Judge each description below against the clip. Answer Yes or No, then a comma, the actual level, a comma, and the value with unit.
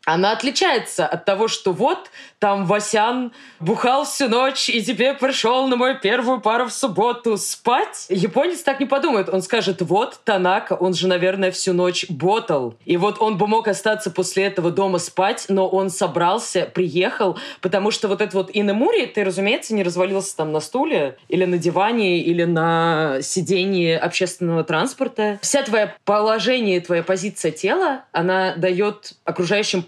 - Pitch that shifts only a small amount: No, average, 3.7 semitones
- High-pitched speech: Yes, high, 200 Hz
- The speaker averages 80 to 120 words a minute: No, fast, 160 wpm